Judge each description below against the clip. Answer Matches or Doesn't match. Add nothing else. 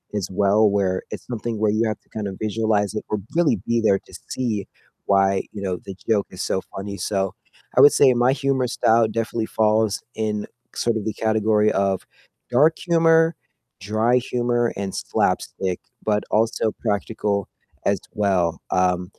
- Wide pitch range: Doesn't match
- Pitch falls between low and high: Doesn't match